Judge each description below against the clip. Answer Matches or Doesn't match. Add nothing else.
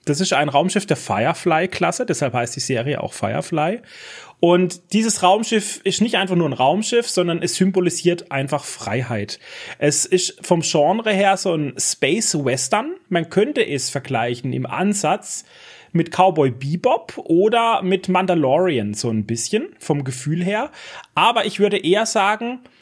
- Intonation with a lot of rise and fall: Matches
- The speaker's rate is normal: Matches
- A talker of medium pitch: Matches